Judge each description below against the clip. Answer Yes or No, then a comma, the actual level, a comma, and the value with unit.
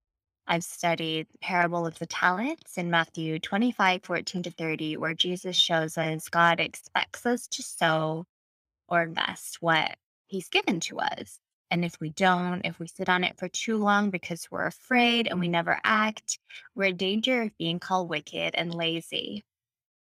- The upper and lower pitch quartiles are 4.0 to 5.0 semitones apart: No, average, 3.5 semitones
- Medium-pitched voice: Yes, medium, 175 Hz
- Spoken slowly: No, average, 170 wpm